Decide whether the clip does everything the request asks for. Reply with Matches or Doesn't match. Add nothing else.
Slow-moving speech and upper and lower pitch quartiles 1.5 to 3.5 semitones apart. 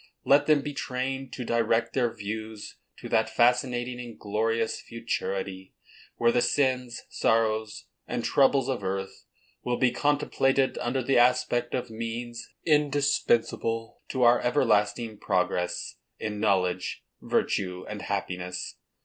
Matches